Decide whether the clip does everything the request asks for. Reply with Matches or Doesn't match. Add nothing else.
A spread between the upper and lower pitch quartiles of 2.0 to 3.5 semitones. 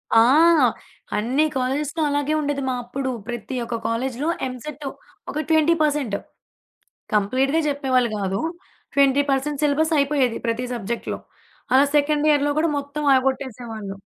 Matches